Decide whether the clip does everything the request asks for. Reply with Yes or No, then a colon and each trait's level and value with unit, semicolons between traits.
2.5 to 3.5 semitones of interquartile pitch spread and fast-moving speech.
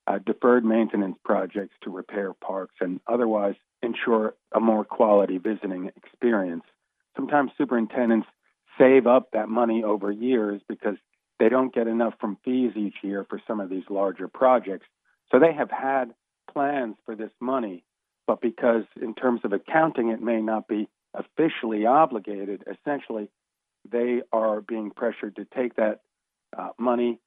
No: average, 3.1 semitones; average, 150 wpm